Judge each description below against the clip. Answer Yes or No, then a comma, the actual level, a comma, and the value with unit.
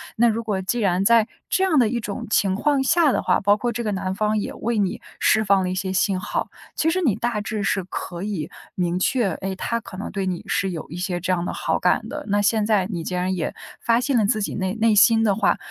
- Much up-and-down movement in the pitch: No, average, 3.4 semitones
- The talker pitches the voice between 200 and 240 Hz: Yes, high, 205 Hz